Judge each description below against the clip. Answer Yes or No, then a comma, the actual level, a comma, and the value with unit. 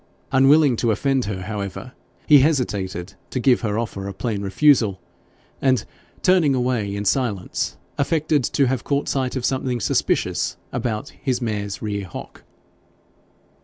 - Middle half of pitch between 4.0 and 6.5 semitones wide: Yes, average, 4.9 semitones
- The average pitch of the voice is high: No, low, 120 Hz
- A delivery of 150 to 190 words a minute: No, average, 140 wpm